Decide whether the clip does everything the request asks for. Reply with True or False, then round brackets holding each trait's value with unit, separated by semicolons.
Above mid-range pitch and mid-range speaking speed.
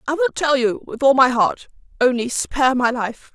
False (260 Hz; 215 wpm)